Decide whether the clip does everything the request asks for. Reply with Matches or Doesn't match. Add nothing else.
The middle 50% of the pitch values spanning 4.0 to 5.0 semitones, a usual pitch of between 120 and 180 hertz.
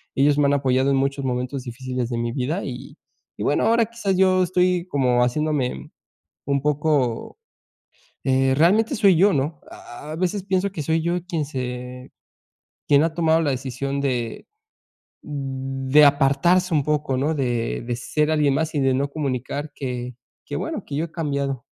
Doesn't match